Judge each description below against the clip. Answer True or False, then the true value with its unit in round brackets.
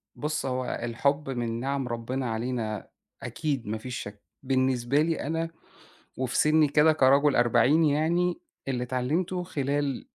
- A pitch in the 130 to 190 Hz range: True (135 Hz)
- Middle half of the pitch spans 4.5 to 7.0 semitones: False (3.8 semitones)